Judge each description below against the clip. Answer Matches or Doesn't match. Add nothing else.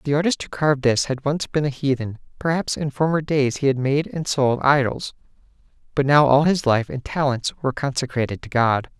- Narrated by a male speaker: Matches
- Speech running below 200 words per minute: Doesn't match